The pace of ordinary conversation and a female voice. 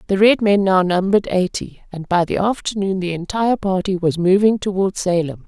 Yes: average, 185 wpm; female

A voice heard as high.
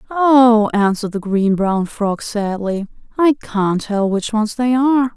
Yes: high, 220 Hz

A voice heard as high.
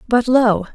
Yes: high, 230 Hz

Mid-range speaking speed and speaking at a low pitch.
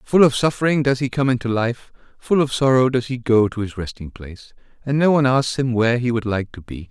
No: fast, 250 wpm; low, 125 Hz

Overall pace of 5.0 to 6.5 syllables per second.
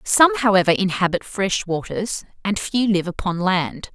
No: 4.6 syllables/s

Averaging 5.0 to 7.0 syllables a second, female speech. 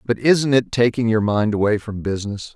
No: 5.3 syllables/s; male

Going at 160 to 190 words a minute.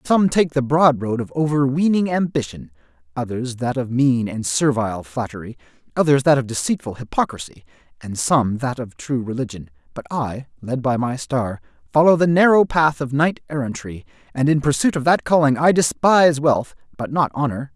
Yes: average, 170 wpm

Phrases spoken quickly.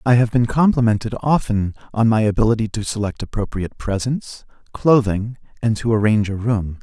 No: average, 160 wpm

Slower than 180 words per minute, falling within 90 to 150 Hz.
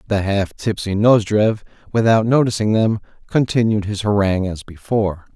Yes: slow, 135 wpm; low, 105 Hz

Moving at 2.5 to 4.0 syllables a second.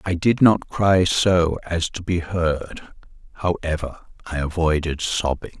Yes: 3.9 syllables/s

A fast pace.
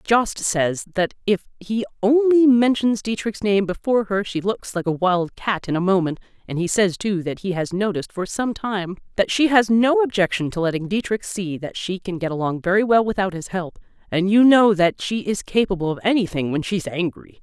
Yes: fast, 215 wpm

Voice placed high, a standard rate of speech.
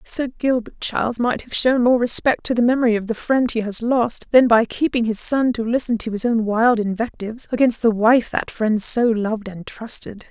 No: high, 230 Hz; fast, 220 wpm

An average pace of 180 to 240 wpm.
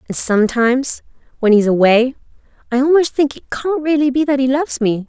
Yes: average, 200 wpm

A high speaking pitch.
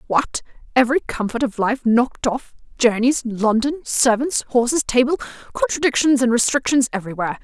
Yes: very high, 250 Hz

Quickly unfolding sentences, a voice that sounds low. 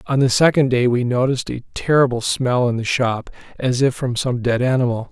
Yes: fast, 210 wpm; low, 125 Hz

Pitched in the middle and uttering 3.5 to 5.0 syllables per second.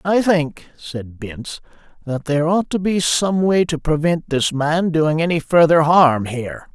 Yes: medium, 160 Hz; 4.3 syllables/s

